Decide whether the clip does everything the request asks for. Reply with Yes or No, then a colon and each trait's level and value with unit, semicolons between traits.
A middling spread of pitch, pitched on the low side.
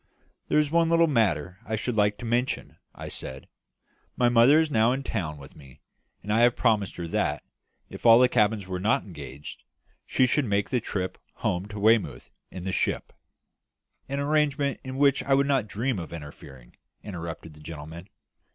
No: wide, 7.3 semitones; low, 110 Hz